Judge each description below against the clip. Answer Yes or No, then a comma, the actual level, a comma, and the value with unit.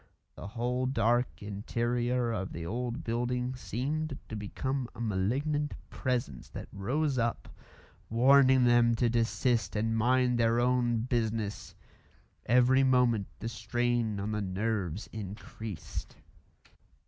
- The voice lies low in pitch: Yes, low, 120 Hz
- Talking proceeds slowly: Yes, slow, 120 wpm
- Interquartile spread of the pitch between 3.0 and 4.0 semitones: No, narrow, 2.5 semitones